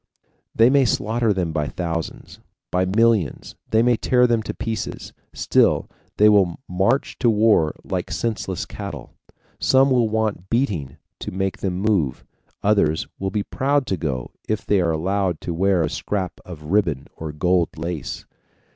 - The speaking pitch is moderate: No, very low, 95 Hz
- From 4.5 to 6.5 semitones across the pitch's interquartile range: Yes, average, 4.8 semitones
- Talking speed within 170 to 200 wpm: No, average, 160 wpm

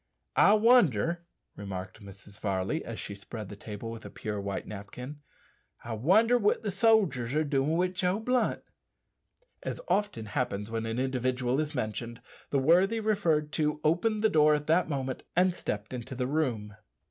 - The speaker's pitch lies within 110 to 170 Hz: Yes, low, 135 Hz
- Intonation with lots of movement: Yes, wide, 8.2 semitones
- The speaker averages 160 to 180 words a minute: Yes, average, 170 wpm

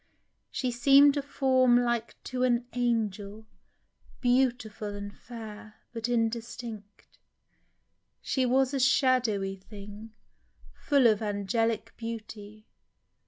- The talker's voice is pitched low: No, high, 230 Hz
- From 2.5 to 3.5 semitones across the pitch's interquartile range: Yes, average, 3.0 semitones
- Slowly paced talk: Yes, slow, 100 wpm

